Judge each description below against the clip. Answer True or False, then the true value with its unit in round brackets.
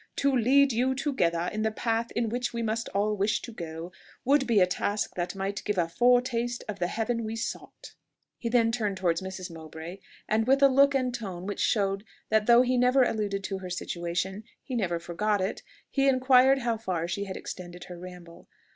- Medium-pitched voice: False (215 Hz)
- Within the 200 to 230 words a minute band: True (205 wpm)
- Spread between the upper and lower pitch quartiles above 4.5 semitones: True (5.0 semitones)